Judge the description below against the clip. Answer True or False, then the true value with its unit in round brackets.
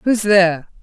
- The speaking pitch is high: True (195 Hz)